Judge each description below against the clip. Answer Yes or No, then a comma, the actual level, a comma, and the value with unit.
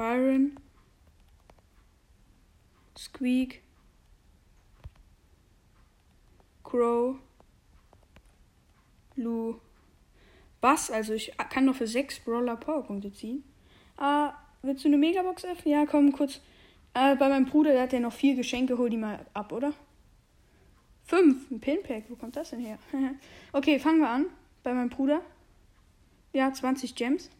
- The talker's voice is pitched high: Yes, very high, 255 Hz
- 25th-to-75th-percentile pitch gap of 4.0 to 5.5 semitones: Yes, average, 4.4 semitones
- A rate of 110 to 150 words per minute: Yes, slow, 125 wpm